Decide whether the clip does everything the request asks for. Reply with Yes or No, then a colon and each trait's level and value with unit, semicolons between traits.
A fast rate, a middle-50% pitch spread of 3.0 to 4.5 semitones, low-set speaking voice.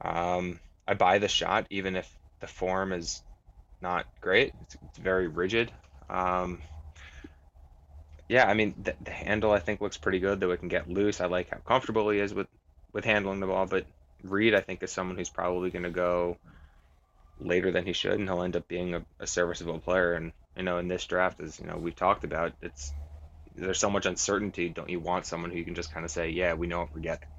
No: fast, 225 wpm; narrow, 2.6 semitones; very low, 90 Hz